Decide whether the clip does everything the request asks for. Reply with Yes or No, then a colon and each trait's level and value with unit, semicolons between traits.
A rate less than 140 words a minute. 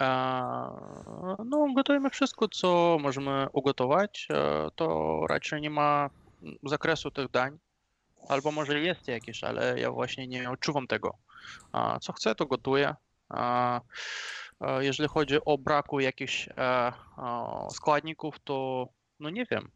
Yes: slow, 110 wpm